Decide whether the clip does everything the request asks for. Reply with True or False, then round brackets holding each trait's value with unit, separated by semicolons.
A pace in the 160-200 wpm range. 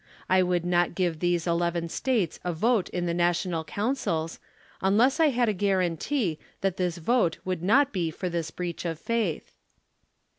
True (170 wpm)